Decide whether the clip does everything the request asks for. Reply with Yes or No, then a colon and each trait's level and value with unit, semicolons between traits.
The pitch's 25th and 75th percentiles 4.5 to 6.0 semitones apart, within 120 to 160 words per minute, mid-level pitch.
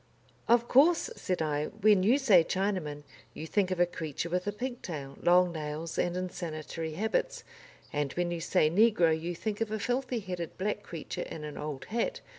No: average, 4.8 semitones; average, 185 wpm; medium, 180 Hz